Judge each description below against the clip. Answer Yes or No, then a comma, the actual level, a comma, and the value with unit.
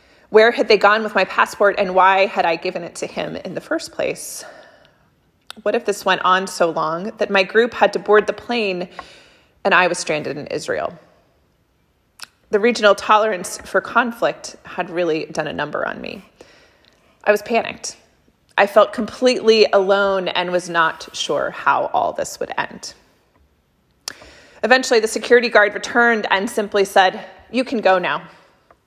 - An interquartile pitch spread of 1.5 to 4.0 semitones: Yes, average, 3.4 semitones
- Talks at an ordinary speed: Yes, average, 165 wpm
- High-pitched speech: Yes, high, 205 Hz